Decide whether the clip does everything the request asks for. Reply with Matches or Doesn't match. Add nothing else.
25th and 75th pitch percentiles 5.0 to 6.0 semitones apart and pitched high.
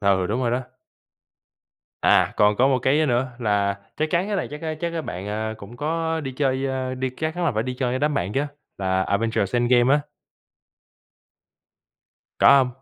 Doesn't match